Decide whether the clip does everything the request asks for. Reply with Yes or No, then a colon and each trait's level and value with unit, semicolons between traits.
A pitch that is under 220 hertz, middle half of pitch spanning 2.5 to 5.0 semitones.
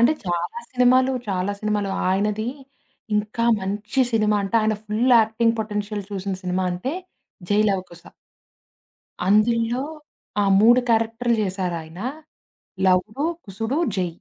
Yes: high, 210 Hz; average, 3.1 semitones